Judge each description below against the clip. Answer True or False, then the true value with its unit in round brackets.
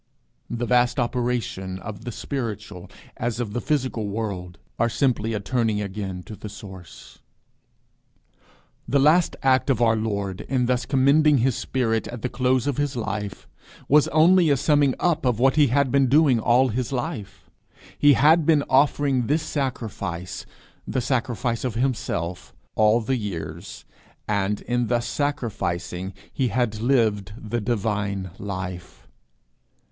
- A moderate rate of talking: True (150 wpm)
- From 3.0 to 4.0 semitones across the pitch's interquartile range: False (4.5 semitones)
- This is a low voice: True (120 Hz)